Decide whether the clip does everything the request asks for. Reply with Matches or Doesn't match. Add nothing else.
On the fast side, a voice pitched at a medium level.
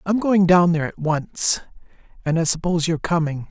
Doesn't match